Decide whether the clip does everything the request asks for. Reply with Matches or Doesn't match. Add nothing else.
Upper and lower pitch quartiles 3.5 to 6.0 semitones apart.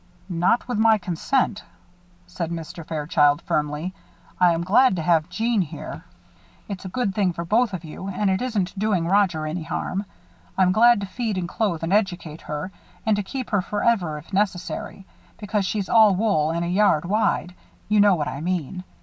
Matches